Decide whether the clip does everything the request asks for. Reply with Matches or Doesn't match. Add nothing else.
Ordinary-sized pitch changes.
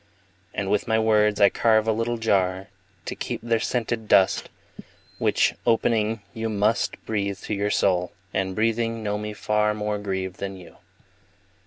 Doesn't match